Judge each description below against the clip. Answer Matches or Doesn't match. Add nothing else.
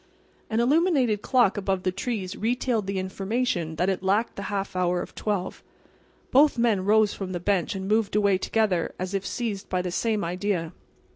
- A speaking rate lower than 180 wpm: Doesn't match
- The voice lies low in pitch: Doesn't match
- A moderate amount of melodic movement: Matches